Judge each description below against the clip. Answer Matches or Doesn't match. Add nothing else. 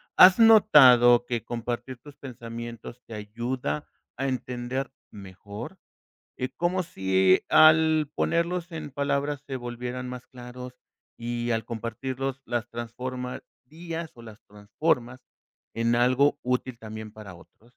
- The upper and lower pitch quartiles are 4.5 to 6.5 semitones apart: Doesn't match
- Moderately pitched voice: Doesn't match